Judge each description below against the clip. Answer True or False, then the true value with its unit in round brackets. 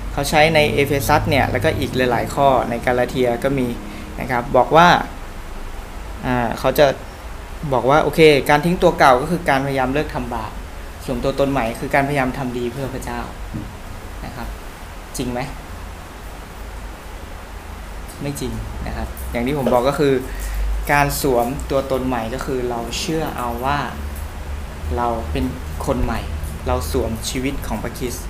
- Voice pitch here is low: True (120 Hz)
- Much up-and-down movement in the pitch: True (8.8 semitones)